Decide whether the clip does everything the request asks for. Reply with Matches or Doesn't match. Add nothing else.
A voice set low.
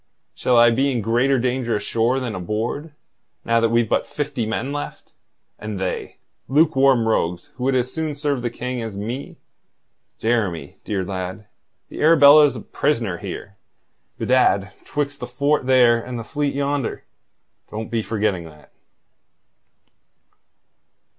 Matches